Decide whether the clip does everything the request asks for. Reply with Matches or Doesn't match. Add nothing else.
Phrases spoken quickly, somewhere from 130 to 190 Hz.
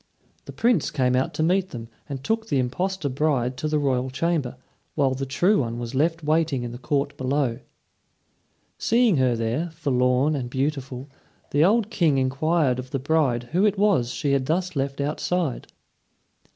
Doesn't match